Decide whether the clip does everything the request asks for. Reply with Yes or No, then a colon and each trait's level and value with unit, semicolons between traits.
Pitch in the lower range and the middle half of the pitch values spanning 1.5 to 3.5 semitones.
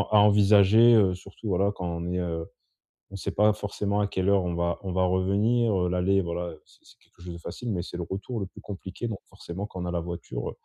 Yes: very low, 95 Hz; average, 2.7 semitones